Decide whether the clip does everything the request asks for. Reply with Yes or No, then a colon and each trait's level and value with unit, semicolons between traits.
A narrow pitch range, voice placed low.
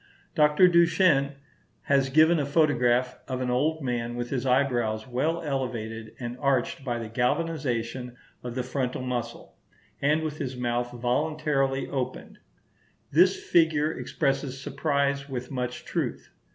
No: average, 3.4 semitones; low, 130 Hz